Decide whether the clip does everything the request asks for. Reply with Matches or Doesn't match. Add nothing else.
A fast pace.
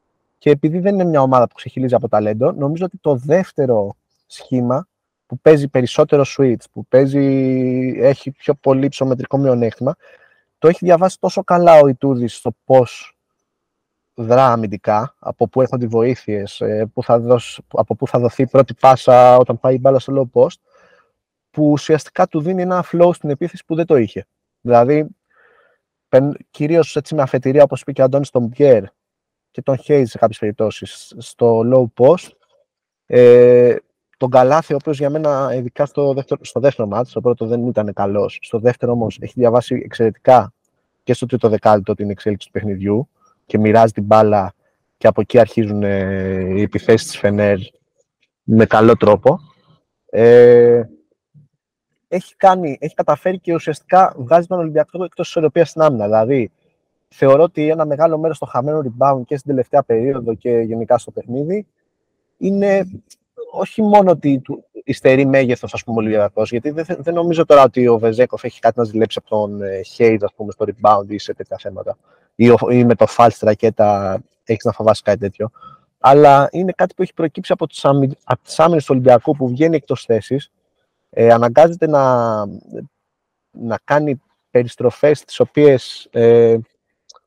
Doesn't match